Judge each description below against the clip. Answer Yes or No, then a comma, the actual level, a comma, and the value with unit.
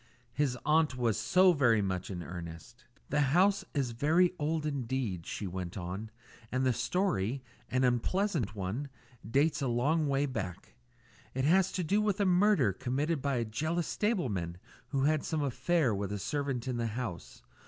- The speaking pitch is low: Yes, low, 130 Hz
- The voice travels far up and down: Yes, wide, 6.2 semitones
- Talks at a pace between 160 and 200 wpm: Yes, average, 170 wpm